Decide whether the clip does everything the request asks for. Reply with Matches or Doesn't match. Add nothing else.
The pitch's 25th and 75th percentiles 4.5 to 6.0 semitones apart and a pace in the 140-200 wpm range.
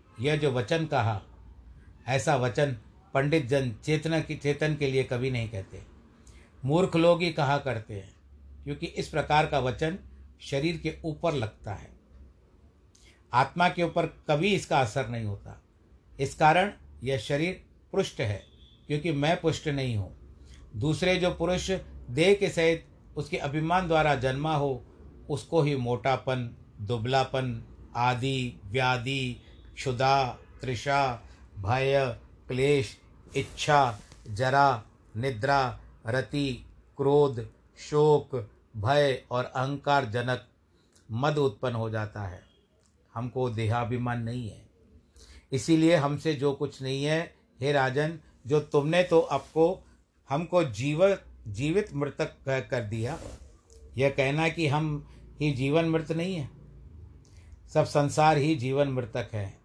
Doesn't match